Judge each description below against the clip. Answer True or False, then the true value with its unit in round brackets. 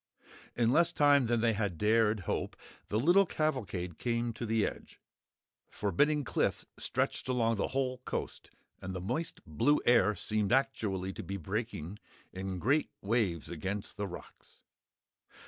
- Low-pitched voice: True (110 Hz)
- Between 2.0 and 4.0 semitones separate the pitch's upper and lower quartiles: False (4.9 semitones)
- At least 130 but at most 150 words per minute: True (145 wpm)